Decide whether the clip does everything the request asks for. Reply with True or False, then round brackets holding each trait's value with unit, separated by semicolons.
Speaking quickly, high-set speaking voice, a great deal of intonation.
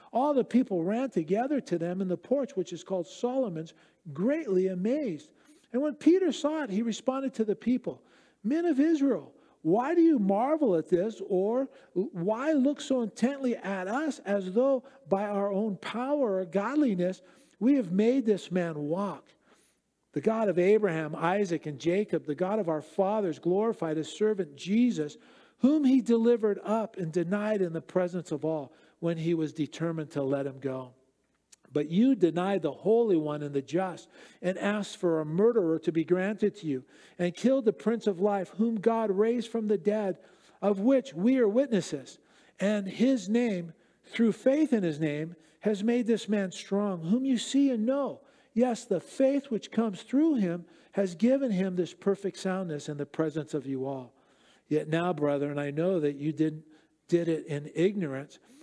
False (180 wpm; 195 Hz; 6.1 semitones)